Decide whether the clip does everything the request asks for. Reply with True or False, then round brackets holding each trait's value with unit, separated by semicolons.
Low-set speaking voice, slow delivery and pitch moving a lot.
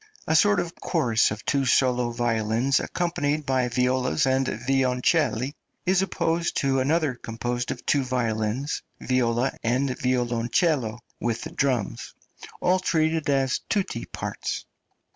False (130 Hz; 125 wpm; 3.9 semitones)